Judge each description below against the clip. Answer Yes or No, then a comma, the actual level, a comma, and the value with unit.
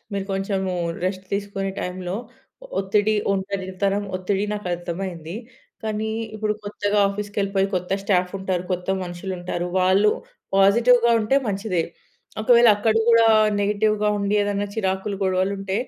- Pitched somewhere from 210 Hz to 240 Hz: No, high, 195 Hz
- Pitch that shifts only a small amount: Yes, narrow, 1.8 semitones